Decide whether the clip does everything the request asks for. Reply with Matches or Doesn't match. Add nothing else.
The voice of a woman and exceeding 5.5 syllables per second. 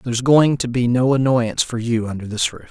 Doesn't match